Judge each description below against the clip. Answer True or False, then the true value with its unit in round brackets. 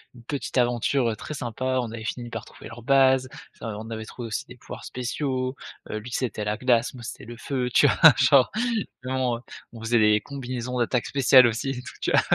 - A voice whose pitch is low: True (120 Hz)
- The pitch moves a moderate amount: False (2.0 semitones)